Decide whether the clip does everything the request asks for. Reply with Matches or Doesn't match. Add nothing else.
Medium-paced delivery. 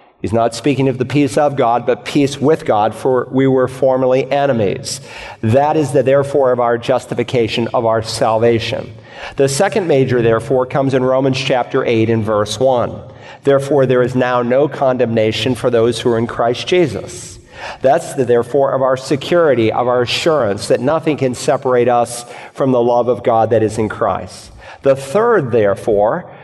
Matches